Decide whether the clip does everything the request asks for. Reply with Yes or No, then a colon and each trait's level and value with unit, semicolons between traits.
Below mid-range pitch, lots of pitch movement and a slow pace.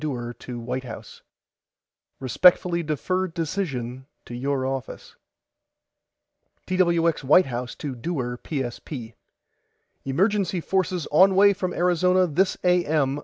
No: medium, 155 Hz; wide, 5.8 semitones; slow, 110 wpm